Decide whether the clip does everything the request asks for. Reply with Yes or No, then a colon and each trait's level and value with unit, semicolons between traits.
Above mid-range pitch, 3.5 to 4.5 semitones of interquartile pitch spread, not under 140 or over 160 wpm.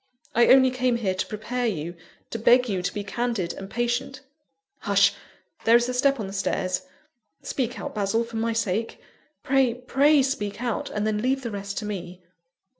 No: high, 230 Hz; average, 3.8 semitones; average, 190 wpm